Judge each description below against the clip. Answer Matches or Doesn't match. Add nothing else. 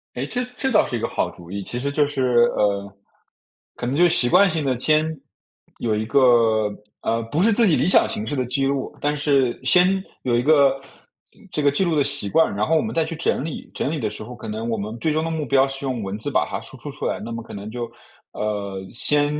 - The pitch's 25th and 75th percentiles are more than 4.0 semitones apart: Matches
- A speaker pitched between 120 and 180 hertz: Matches